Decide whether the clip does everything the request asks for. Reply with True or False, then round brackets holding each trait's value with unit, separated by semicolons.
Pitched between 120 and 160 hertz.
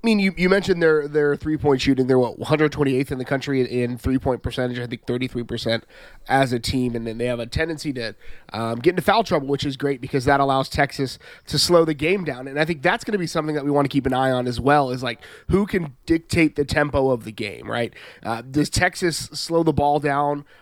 True (140 Hz)